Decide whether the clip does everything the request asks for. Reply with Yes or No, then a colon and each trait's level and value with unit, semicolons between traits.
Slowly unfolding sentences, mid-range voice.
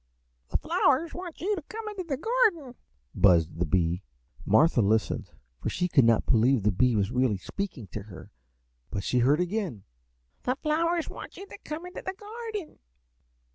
No: average, 175 wpm; medium, 180 Hz